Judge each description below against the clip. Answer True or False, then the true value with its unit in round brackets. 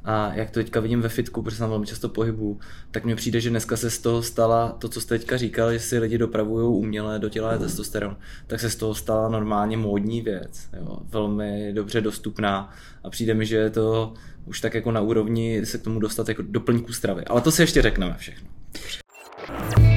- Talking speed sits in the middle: False (205 wpm)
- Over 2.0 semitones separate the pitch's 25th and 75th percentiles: False (1.3 semitones)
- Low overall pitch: True (110 Hz)